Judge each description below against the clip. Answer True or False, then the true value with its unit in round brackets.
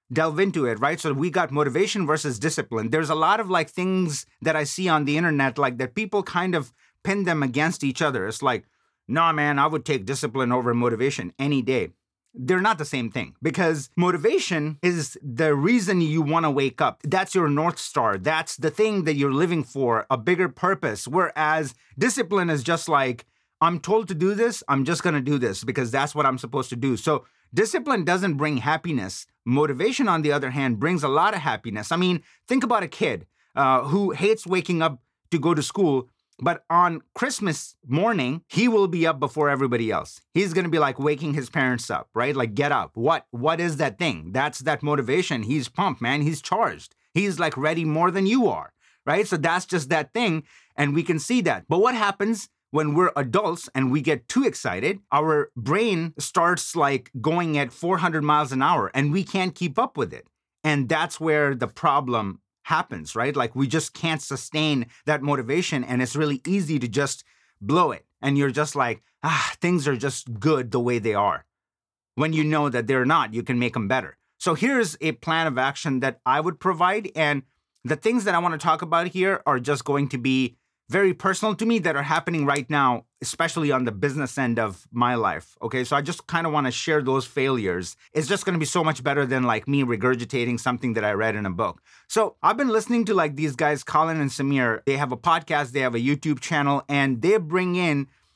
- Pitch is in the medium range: True (150 Hz)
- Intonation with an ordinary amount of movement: True (4.6 semitones)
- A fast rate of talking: True (215 wpm)